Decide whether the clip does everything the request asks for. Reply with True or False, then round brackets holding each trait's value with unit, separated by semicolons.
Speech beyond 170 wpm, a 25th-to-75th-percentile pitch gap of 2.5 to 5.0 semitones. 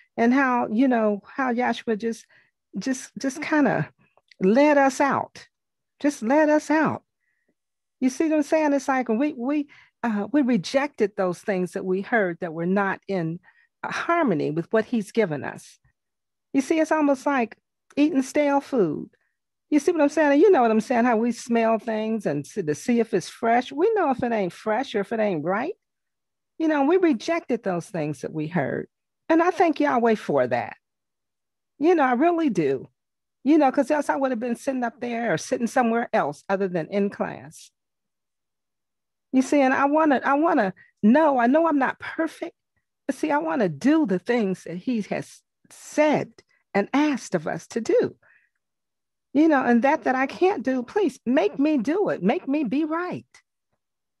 False (190 wpm; 5.5 semitones)